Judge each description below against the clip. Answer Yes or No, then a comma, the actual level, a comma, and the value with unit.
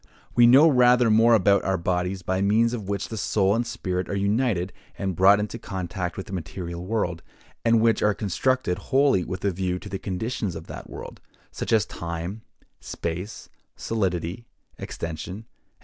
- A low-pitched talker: Yes, low, 100 Hz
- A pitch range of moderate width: Yes, average, 3.8 semitones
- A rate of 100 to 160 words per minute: No, average, 175 wpm